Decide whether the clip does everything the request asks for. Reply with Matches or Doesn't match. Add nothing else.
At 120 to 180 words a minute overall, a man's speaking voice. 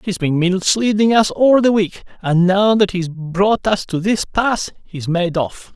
Doesn't match